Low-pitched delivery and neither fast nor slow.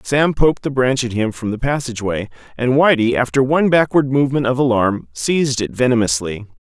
Yes: low, 125 Hz; average, 180 wpm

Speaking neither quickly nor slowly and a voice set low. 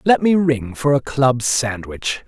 Yes: average, 185 wpm; low, 130 Hz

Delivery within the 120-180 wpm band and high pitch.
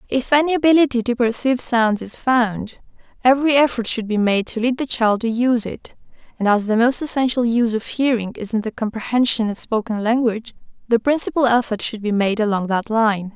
No: average, 200 wpm; high, 235 Hz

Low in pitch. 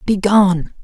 No: high, 195 Hz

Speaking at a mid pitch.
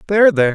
Yes: medium, 170 Hz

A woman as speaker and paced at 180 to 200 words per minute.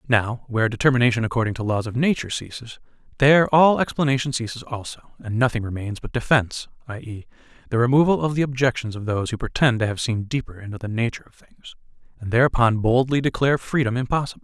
No: male; average, 185 wpm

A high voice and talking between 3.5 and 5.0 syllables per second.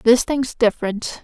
Yes: high, 235 Hz; 4.5 syllables/s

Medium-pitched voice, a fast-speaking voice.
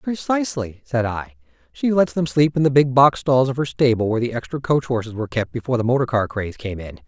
No: low, 125 Hz; fast, 245 wpm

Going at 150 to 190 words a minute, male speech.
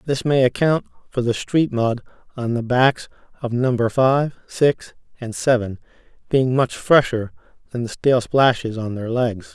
Yes: average, 165 wpm; male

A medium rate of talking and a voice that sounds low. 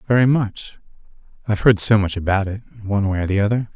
Yes: average, 190 wpm; low, 105 Hz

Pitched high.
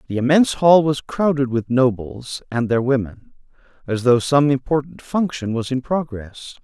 No: low, 130 Hz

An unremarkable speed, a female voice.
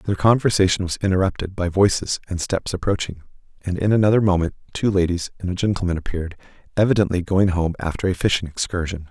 No: average, 170 wpm; male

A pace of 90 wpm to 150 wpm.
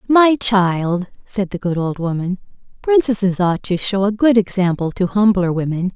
No: average, 170 wpm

